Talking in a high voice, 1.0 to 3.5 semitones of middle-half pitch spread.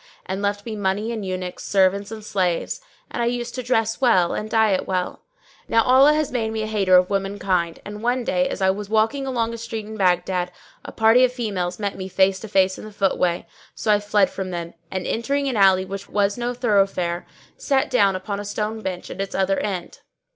Yes: high, 205 Hz; average, 3.1 semitones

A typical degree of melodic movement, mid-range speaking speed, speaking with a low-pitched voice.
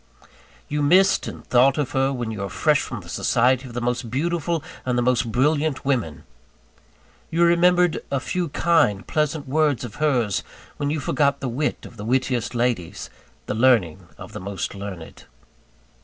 Yes: average, 4.4 semitones; average, 170 wpm; low, 130 Hz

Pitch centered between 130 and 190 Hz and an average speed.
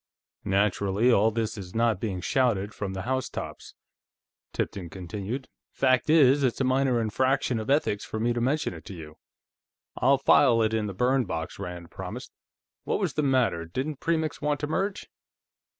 No: low, 115 Hz; average, 170 wpm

